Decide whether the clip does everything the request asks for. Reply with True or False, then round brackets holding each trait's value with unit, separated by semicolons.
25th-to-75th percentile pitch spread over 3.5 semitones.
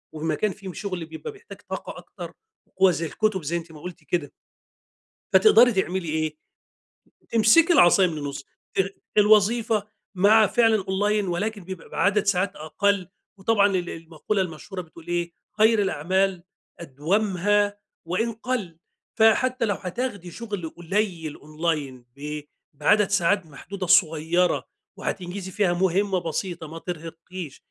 True (3.9 semitones)